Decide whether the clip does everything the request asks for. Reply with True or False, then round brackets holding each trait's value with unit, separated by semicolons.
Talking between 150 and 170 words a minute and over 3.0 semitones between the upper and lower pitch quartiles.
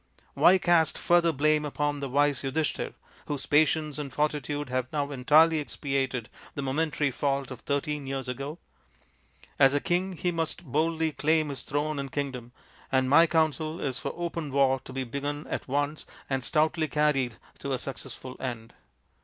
False (165 wpm; 2.6 semitones)